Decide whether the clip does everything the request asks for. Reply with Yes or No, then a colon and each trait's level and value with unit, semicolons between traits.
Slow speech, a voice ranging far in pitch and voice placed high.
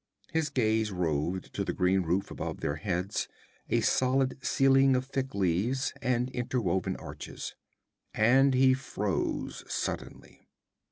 No: slow, 125 wpm; wide, 5.8 semitones; low, 115 Hz